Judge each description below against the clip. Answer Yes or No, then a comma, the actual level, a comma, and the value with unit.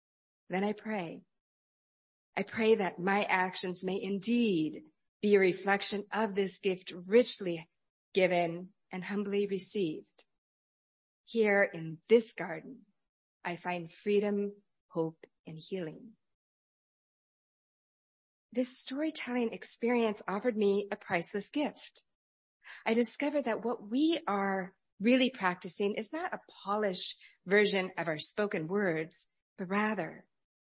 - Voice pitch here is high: Yes, high, 200 Hz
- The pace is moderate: No, slow, 115 wpm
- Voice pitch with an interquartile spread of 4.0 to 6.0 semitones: No, average, 3.3 semitones